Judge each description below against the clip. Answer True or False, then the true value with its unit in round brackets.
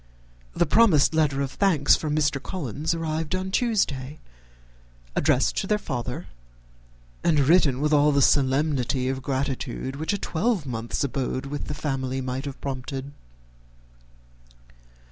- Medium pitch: True (145 Hz)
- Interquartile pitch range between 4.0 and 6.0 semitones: False (3.2 semitones)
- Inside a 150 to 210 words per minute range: False (135 wpm)